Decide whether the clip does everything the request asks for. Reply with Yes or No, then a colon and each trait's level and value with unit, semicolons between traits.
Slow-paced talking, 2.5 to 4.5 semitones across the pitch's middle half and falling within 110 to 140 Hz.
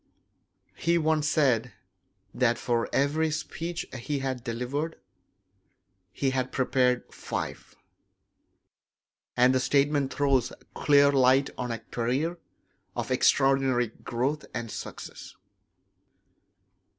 Yes: slow, 100 wpm; average, 2.8 semitones; low, 135 Hz